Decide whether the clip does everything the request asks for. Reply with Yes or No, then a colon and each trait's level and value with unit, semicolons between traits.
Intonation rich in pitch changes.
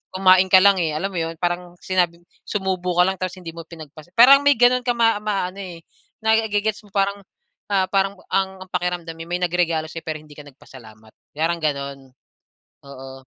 No: average, 3.3 semitones